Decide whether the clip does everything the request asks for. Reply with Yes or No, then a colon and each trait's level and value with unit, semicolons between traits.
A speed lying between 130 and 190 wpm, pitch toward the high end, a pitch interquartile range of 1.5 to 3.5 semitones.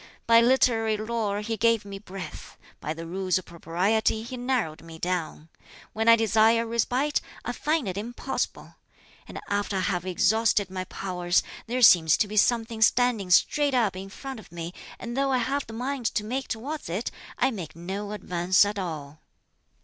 No: average, 180 wpm; high, 215 Hz; average, 4.2 semitones